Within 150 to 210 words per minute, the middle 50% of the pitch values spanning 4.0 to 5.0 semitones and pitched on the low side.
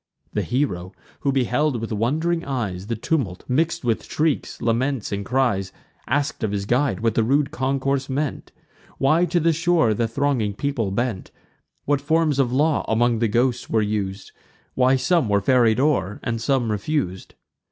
Yes: average, 165 wpm; average, 4.6 semitones; low, 125 Hz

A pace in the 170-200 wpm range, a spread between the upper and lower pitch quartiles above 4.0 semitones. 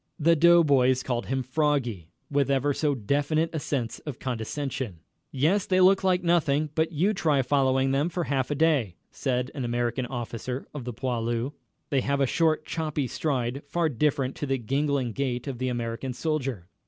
No: average, 180 wpm; average, 3.5 semitones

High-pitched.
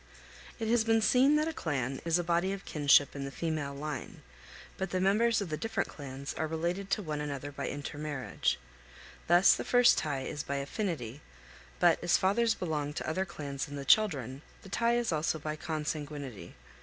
No: medium, 155 Hz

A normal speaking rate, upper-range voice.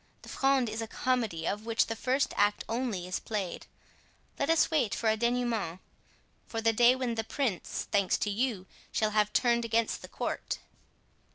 Yes: average, 175 wpm; high, 225 Hz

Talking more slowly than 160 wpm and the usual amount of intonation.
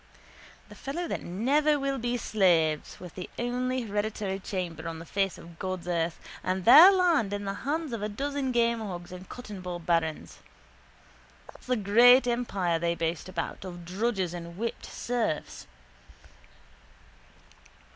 No: average, 145 wpm; wide, 5.8 semitones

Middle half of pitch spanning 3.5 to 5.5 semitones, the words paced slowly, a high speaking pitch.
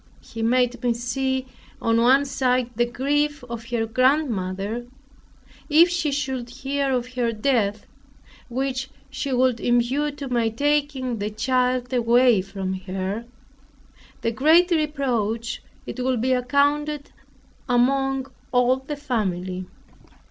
No: average, 2.9 semitones; slow, 125 wpm; very high, 250 Hz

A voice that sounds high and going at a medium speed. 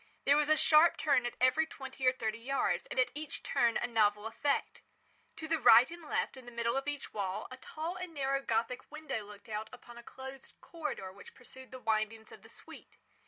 No: very high, 255 Hz; fast, 215 wpm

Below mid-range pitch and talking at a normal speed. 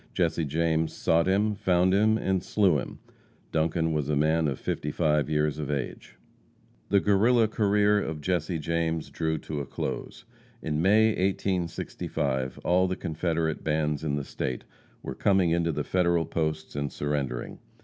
Yes: very low, 80 Hz; average, 155 wpm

